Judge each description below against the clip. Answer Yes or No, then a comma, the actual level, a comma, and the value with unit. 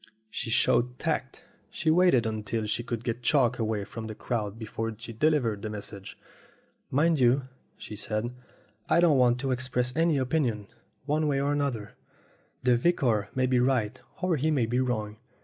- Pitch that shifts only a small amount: No, average, 3.9 semitones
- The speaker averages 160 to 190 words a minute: Yes, average, 175 wpm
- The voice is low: Yes, low, 125 Hz